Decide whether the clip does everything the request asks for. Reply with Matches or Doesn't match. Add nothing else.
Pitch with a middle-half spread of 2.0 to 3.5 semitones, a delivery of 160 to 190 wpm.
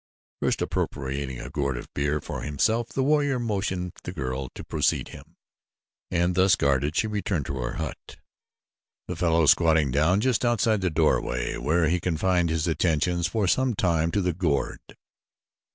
Doesn't match